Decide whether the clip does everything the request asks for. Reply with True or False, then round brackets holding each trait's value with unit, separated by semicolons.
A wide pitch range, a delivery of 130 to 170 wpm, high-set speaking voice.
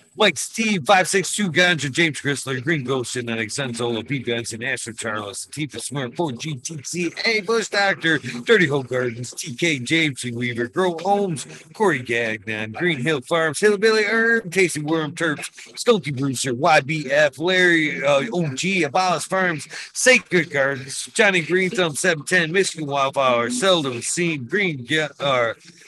False (5.7 semitones; 140 wpm; 155 Hz)